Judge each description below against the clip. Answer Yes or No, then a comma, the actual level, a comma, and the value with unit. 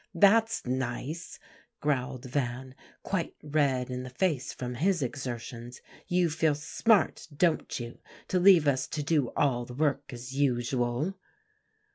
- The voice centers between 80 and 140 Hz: Yes, low, 135 Hz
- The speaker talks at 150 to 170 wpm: No, slow, 135 wpm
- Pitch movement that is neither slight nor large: Yes, average, 4.3 semitones